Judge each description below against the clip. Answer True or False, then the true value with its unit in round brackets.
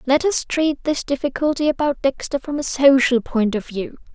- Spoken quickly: False (190 wpm)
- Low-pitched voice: False (275 Hz)